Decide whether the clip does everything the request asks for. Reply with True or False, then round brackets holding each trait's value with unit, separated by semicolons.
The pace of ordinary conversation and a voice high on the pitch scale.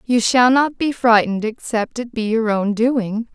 True (195 wpm; 230 Hz)